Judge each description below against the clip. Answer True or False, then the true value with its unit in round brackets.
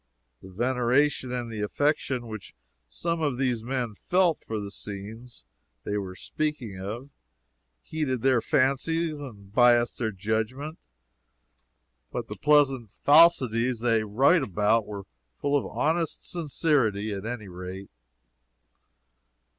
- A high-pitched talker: False (120 Hz)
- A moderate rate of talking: False (120 wpm)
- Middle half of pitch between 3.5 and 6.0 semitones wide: True (5.3 semitones)